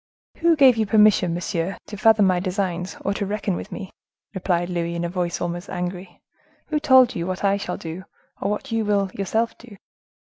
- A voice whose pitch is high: Yes, high, 195 Hz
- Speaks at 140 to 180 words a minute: No, average, 195 wpm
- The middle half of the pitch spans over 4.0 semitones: No, average, 3.3 semitones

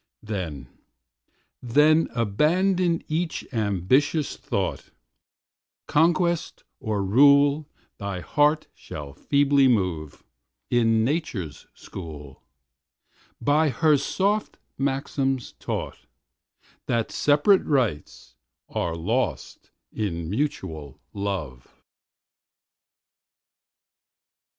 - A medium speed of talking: No, slow, 75 wpm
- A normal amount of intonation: No, wide, 7.8 semitones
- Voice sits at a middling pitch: No, low, 130 Hz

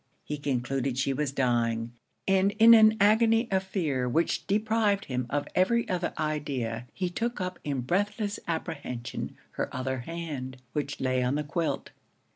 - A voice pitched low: No, medium, 150 Hz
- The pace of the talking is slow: No, average, 155 wpm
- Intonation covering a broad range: Yes, wide, 7.3 semitones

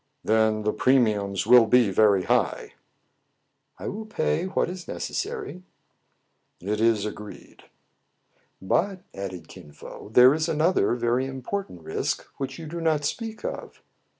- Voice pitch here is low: Yes, low, 125 Hz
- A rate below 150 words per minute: Yes, average, 140 wpm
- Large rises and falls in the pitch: Yes, wide, 7.8 semitones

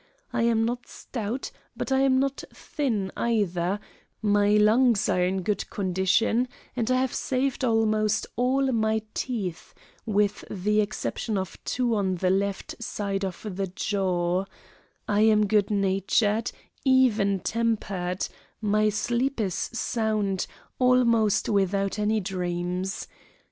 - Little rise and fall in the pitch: No, average, 3.2 semitones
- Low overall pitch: No, high, 210 Hz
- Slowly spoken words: Yes, slow, 130 wpm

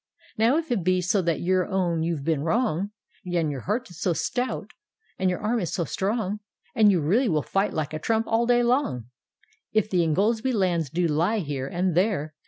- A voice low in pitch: No, medium, 185 Hz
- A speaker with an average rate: No, fast, 215 wpm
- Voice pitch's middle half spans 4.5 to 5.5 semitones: Yes, average, 5.2 semitones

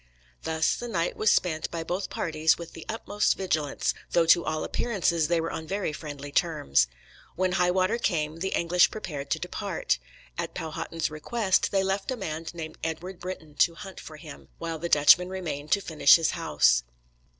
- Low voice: No, medium, 165 Hz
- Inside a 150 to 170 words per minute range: No, average, 185 wpm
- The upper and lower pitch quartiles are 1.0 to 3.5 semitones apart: Yes, average, 3.1 semitones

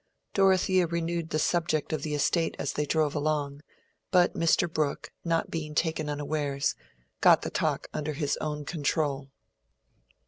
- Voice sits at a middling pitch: Yes, medium, 155 Hz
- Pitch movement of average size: No, narrow, 2.2 semitones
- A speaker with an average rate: Yes, average, 145 wpm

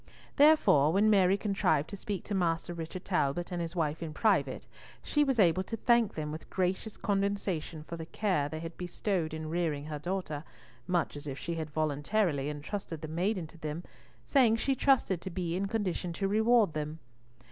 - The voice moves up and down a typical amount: Yes, average, 4.3 semitones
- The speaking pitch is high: No, medium, 175 Hz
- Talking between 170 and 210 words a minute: Yes, average, 190 wpm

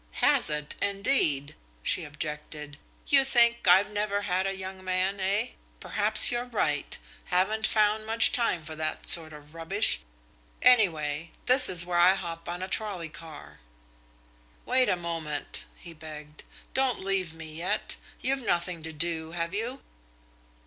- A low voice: No, medium, 180 Hz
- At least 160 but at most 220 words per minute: No, average, 150 wpm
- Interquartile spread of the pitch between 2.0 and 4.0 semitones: No, average, 4.9 semitones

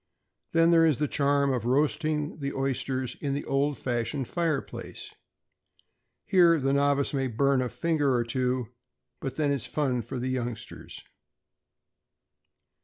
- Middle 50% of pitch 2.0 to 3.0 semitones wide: Yes, average, 2.7 semitones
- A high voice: No, medium, 140 Hz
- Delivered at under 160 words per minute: Yes, average, 145 wpm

